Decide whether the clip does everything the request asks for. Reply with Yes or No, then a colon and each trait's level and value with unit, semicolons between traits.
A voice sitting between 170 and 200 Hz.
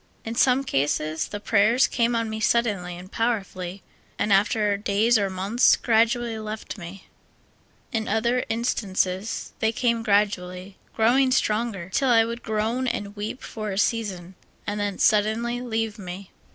No: high, 215 Hz